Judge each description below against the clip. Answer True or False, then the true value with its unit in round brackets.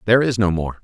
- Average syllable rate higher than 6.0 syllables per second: True (7.5 syllables/s)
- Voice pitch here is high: False (100 Hz)